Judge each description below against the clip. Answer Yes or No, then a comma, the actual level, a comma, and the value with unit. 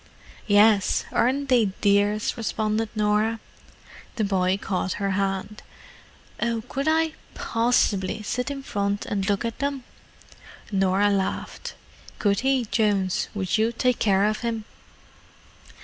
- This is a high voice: Yes, high, 215 Hz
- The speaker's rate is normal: No, slow, 115 wpm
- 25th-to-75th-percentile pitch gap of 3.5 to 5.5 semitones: No, average, 2.8 semitones